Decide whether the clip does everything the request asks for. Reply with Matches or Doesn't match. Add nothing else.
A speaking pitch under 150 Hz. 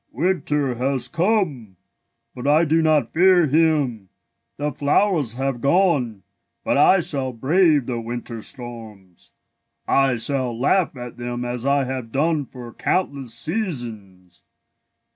Matches